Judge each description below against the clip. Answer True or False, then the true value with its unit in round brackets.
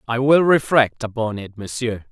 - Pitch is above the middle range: False (120 Hz)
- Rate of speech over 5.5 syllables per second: False (4.6 syllables/s)